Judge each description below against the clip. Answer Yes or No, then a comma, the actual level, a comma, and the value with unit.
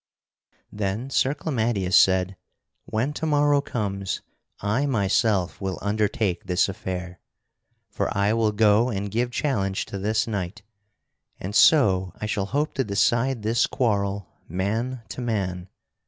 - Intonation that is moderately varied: Yes, average, 3.6 semitones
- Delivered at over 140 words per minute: No, slow, 135 wpm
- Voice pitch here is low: Yes, low, 105 Hz